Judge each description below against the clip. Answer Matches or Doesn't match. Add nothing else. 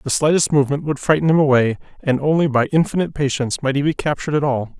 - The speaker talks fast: Matches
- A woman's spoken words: Doesn't match